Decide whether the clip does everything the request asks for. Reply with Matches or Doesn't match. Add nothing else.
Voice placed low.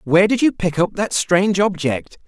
Doesn't match